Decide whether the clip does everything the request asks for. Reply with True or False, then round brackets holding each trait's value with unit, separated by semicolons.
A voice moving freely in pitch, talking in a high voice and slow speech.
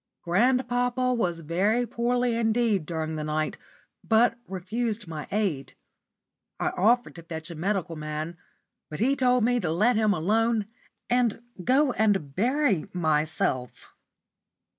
True (6.6 semitones; 210 Hz; 130 wpm)